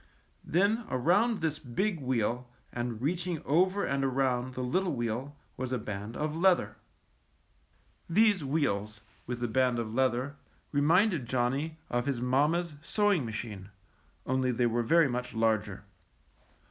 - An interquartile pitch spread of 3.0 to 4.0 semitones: No, wide, 5.4 semitones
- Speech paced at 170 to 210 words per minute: No, average, 145 wpm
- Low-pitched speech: Yes, low, 130 Hz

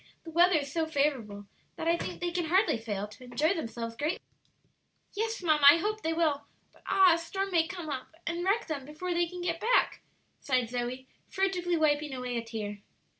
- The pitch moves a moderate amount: No, wide, 5.7 semitones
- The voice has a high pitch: Yes, very high, 320 Hz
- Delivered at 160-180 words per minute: No, average, 195 wpm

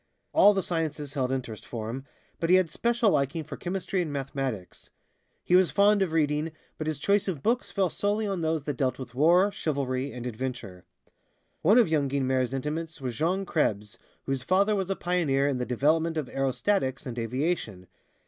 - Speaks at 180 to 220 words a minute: Yes, average, 185 wpm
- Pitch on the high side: No, medium, 150 Hz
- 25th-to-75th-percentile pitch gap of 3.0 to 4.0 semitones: No, wide, 5.6 semitones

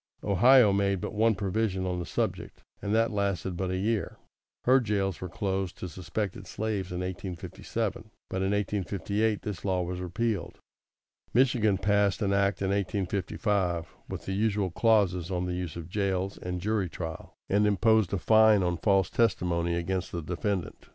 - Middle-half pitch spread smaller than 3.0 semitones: Yes, narrow, 2.5 semitones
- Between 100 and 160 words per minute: No, average, 170 wpm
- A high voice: No, very low, 95 Hz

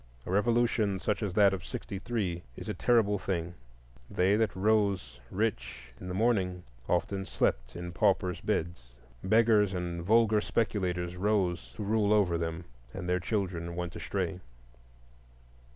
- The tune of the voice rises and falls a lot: No, average, 3.2 semitones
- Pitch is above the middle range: No, very low, 95 Hz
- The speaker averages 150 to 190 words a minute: No, average, 140 wpm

